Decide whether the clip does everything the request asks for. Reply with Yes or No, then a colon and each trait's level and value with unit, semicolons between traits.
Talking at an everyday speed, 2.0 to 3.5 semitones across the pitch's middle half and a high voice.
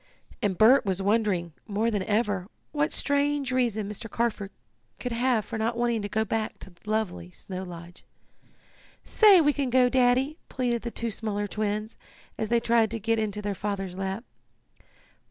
Yes: average, 170 wpm; average, 3.1 semitones; high, 220 Hz